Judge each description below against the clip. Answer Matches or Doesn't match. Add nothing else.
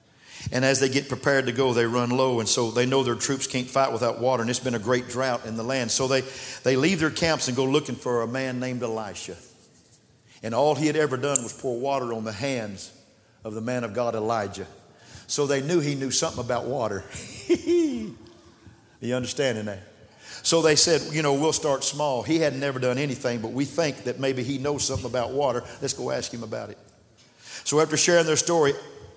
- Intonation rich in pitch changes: Doesn't match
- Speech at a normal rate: Doesn't match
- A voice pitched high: Doesn't match